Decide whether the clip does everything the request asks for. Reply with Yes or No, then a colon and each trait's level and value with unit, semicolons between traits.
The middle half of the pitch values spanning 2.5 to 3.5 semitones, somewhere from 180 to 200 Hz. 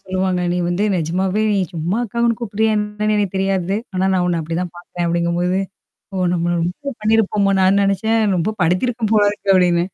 Yes: average, 3.0 semitones; high, 190 Hz